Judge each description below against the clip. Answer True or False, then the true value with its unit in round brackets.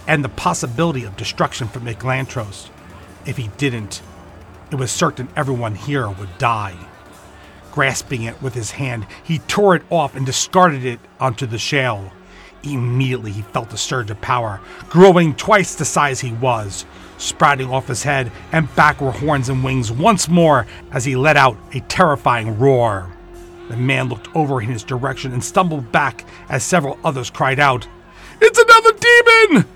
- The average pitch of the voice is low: True (130 Hz)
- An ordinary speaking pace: True (165 wpm)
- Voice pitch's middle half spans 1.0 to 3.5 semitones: False (5.4 semitones)